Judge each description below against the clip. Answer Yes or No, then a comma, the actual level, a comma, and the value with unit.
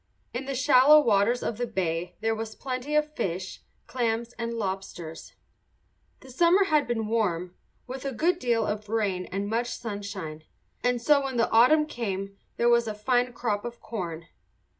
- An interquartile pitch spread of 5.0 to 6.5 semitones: No, average, 3.9 semitones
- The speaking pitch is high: Yes, high, 230 Hz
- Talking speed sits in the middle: Yes, average, 170 wpm